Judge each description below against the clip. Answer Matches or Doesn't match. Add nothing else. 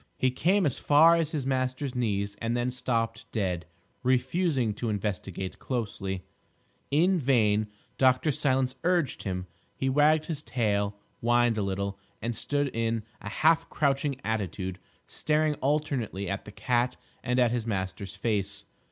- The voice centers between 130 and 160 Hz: Doesn't match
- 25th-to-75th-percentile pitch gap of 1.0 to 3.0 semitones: Doesn't match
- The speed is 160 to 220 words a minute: Doesn't match